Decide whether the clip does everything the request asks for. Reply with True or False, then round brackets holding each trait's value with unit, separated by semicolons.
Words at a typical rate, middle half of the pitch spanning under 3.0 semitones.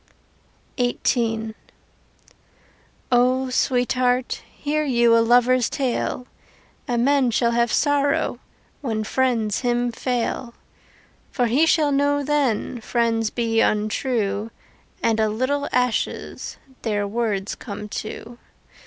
False (105 wpm; 2.4 semitones)